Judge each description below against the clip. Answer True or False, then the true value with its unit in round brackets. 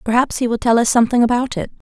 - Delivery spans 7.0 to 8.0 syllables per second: True (7.4 syllables/s)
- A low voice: False (235 Hz)